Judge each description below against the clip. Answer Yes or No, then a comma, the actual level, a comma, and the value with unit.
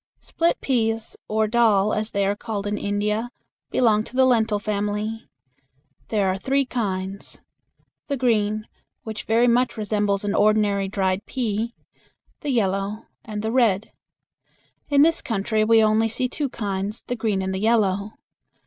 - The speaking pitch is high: Yes, high, 215 Hz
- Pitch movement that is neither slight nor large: No, narrow, 2.3 semitones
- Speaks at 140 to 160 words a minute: Yes, average, 150 wpm